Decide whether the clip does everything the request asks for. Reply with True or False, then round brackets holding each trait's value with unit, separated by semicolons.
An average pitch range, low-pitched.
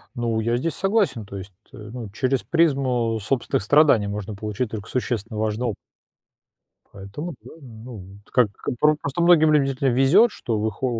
True (4.5 semitones; 120 Hz)